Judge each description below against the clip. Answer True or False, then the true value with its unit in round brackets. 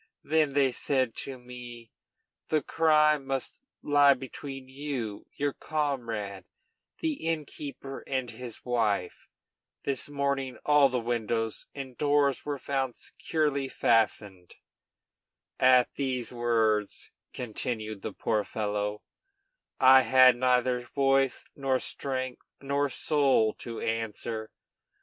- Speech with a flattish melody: False (3.3 semitones)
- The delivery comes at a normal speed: False (110 wpm)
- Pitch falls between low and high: False (130 Hz)